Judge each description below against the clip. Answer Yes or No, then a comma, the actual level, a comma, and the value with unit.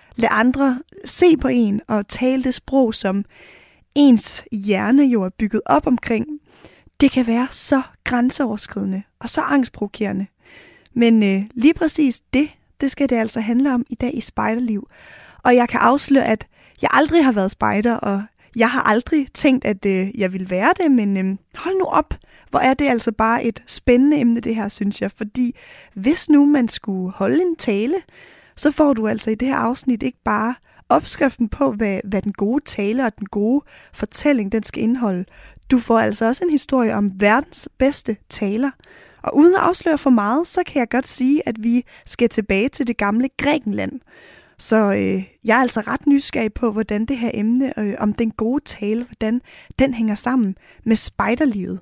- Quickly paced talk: No, average, 185 wpm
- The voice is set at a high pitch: Yes, high, 240 Hz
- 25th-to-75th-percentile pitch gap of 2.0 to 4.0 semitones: No, average, 4.4 semitones